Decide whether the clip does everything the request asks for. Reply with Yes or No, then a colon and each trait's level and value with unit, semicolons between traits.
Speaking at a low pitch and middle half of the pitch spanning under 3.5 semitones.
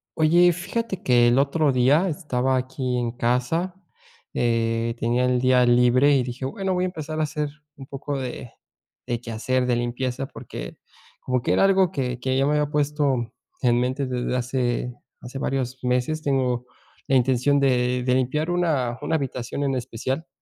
Yes: low, 130 Hz; average, 2.9 semitones